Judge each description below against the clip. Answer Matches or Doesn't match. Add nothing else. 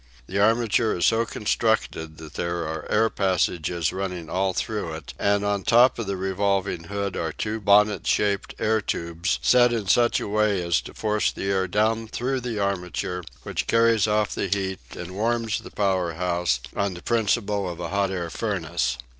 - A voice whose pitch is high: Doesn't match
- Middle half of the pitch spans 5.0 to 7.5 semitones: Doesn't match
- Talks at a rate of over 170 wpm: Matches